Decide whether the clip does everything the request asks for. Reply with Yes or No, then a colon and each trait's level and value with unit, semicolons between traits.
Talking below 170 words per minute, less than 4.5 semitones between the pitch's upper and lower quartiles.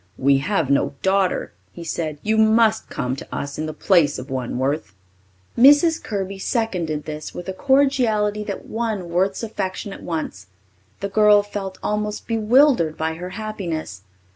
No: average, 160 wpm; wide, 5.6 semitones